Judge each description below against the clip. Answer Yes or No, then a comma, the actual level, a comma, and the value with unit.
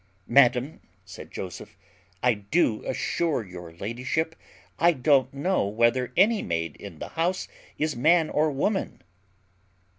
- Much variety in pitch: Yes, wide, 7.1 semitones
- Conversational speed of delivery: No, slow, 125 wpm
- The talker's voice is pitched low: Yes, low, 130 Hz